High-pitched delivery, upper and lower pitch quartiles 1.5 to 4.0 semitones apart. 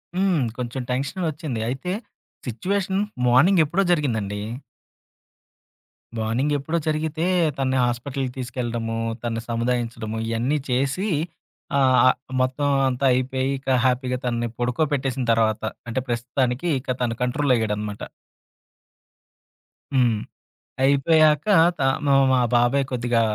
No: low, 130 Hz; average, 3.3 semitones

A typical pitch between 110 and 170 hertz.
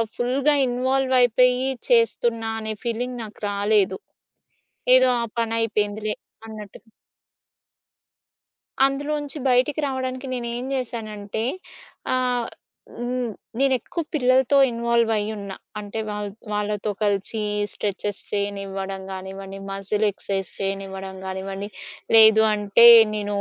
No: high, 220 Hz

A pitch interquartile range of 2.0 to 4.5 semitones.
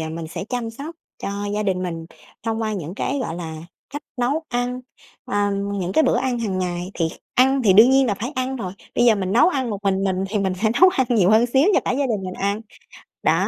No: average, 5.1 semitones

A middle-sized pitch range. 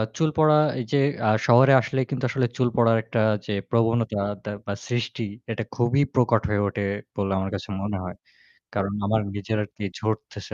Yes: average, 3.0 semitones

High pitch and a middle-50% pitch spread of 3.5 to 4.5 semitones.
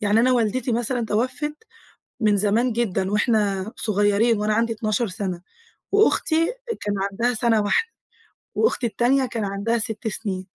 No: high, 220 Hz; average, 2.8 semitones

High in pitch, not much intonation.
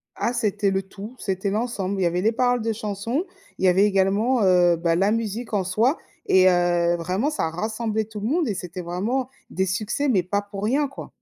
No: high, 205 Hz; average, 3.7 semitones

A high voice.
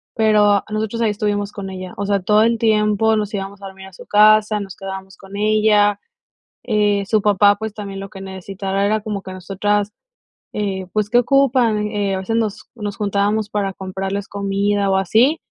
Yes: high, 205 Hz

